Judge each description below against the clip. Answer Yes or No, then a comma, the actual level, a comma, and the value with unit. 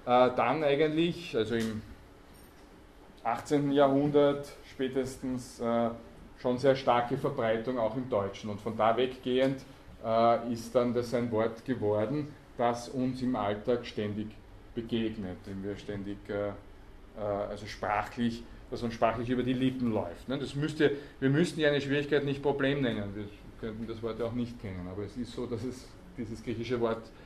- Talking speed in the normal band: Yes, average, 165 wpm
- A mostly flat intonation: No, average, 3.9 semitones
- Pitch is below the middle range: Yes, low, 120 Hz